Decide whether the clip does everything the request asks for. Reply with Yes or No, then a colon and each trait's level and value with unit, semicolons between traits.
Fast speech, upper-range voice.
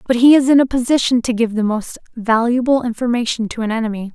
Yes: fast, 215 wpm; high, 235 Hz